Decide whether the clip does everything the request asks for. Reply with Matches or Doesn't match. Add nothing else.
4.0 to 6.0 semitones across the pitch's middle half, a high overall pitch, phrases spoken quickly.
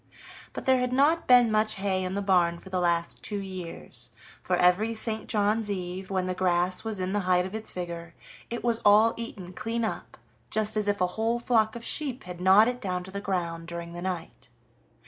Doesn't match